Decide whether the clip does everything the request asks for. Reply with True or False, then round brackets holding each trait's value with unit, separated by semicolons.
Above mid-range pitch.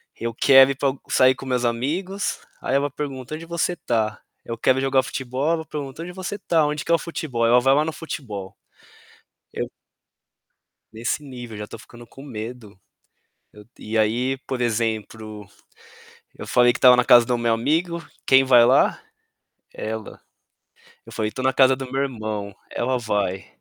False (125 Hz)